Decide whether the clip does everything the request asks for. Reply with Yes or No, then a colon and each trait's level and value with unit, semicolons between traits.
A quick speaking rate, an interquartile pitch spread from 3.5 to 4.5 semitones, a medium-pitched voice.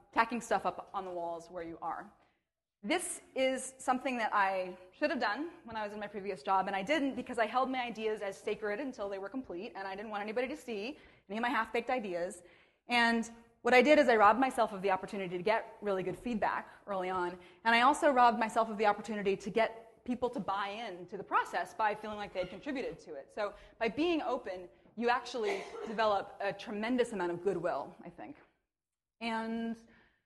No: fast, 215 wpm; average, 3.9 semitones; high, 220 Hz